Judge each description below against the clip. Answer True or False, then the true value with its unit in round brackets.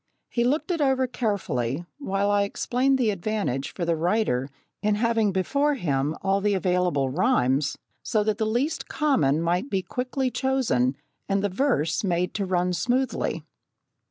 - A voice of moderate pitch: False (200 Hz)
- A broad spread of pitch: True (6.6 semitones)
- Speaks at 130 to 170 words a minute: True (155 wpm)